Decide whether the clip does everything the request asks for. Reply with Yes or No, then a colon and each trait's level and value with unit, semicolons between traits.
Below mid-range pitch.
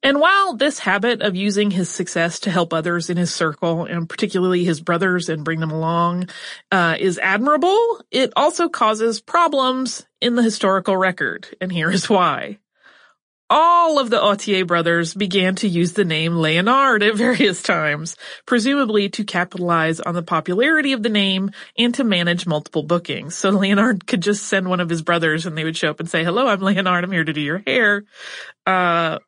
No: high, 190 Hz